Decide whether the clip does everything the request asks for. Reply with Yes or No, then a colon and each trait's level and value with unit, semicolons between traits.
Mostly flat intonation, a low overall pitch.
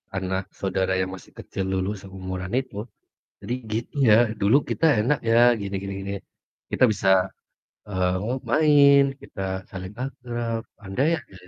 No: average, 4.2 semitones; low, 100 Hz